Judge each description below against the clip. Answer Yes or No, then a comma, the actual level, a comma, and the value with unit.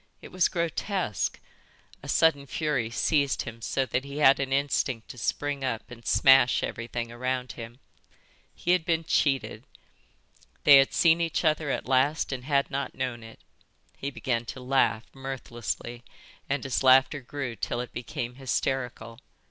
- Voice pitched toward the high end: No, low, 135 Hz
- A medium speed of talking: Yes, average, 155 wpm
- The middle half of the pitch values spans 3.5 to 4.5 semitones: No, average, 2.9 semitones